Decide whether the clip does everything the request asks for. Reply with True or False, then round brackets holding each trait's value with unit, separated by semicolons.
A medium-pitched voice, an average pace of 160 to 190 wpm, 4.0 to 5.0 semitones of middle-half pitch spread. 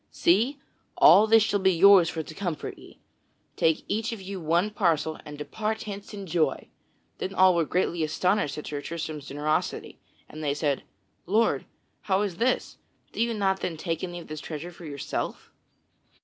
True (175 Hz; 180 wpm; 4.5 semitones)